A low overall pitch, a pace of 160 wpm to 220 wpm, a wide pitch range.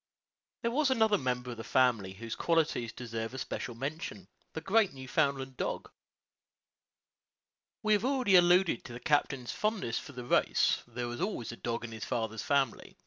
Yes: low, 130 Hz; average, 165 wpm; wide, 7.8 semitones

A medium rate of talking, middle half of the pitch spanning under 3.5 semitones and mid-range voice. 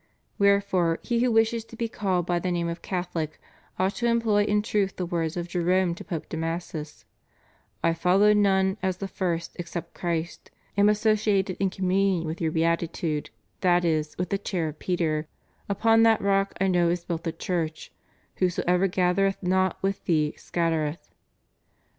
Yes: average, 165 wpm; average, 2.9 semitones; medium, 180 Hz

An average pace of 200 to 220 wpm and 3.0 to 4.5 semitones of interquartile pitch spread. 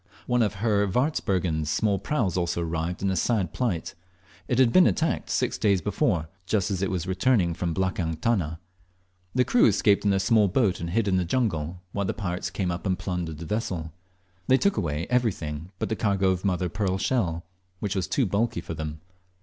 Yes: fast, 205 wpm; average, 4.1 semitones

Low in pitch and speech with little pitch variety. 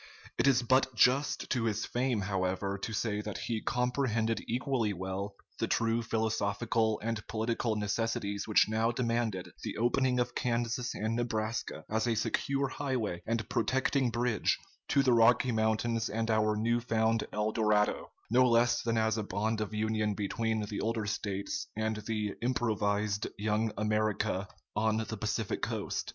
Yes: low, 110 Hz; narrow, 1.9 semitones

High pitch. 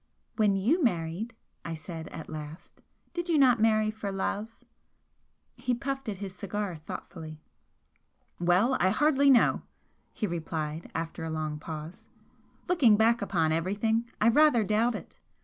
Yes: high, 205 Hz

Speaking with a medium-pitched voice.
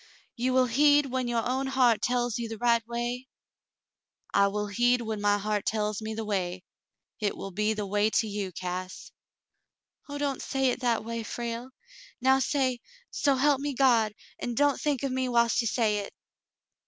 No: high, 235 Hz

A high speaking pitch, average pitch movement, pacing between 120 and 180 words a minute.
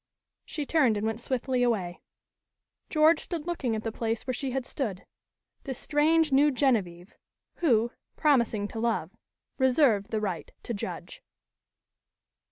Yes: high, 245 Hz; average, 4.8 semitones; average, 140 wpm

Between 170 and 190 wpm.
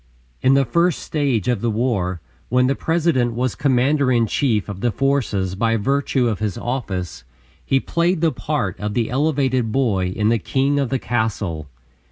Yes: average, 180 wpm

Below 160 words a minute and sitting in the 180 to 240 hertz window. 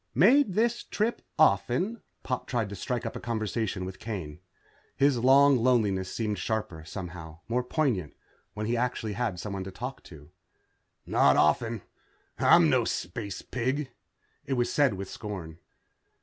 No: average, 150 wpm; low, 115 Hz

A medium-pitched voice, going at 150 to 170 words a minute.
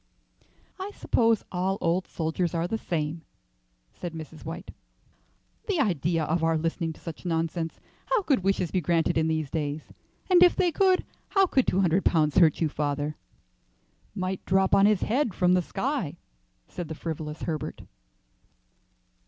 Yes: medium, 170 Hz; average, 160 wpm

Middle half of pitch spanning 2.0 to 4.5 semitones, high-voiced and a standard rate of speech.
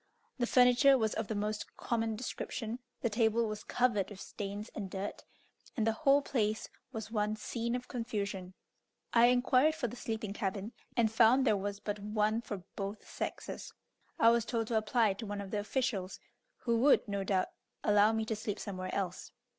Yes: narrow, 2.5 semitones; high, 220 Hz; average, 185 wpm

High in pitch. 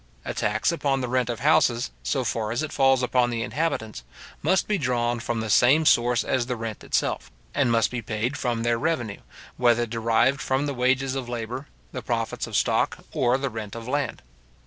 No: low, 125 Hz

